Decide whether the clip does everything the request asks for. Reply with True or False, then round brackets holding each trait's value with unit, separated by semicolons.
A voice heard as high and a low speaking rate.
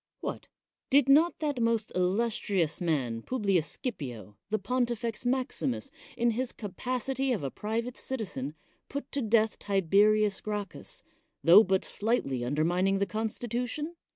True (215 Hz; 130 wpm)